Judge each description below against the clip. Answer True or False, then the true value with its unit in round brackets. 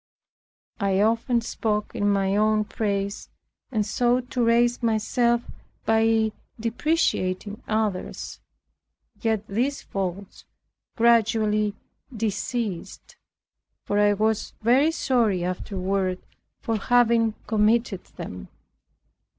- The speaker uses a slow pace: True (95 wpm)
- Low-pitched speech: False (220 Hz)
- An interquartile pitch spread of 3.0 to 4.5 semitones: False (2.6 semitones)